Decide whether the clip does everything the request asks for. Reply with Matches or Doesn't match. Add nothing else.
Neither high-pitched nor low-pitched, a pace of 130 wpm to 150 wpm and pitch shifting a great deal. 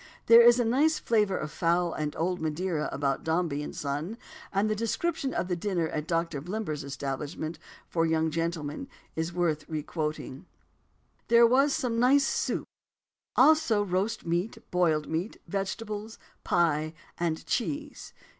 Matches